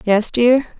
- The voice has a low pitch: No, high, 235 Hz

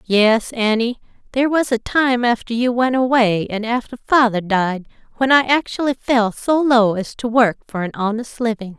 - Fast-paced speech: No, average, 185 wpm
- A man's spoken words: No, female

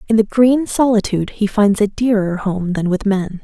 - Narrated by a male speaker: No, female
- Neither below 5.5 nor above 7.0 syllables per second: No, 4.9 syllables/s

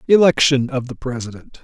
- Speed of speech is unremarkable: Yes, average, 145 wpm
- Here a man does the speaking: Yes, male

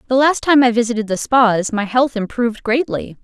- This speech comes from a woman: Yes, female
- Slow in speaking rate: No, fast, 205 wpm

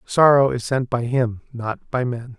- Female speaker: No, male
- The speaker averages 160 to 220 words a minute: Yes, average, 200 wpm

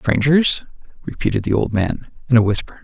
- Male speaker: Yes, male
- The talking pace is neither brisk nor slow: Yes, average, 170 wpm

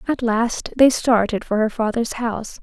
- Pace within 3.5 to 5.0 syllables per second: Yes, 4.5 syllables/s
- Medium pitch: No, high, 230 Hz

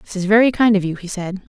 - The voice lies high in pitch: Yes, high, 200 Hz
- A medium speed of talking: No, fast, 310 wpm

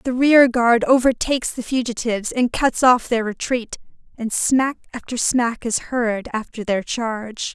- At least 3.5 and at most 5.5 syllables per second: Yes, 4.4 syllables/s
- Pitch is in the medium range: No, high, 240 Hz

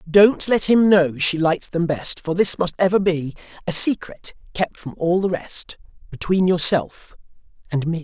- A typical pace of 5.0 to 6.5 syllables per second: No, 4.5 syllables/s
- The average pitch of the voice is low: No, medium, 175 Hz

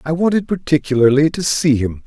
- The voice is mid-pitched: Yes, medium, 150 Hz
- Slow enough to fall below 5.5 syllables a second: No, 5.6 syllables/s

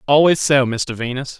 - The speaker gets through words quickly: No, average, 175 wpm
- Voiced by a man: Yes, male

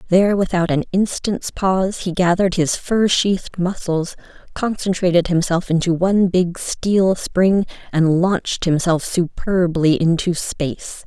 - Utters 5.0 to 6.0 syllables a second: No, 4.3 syllables/s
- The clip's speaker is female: Yes, female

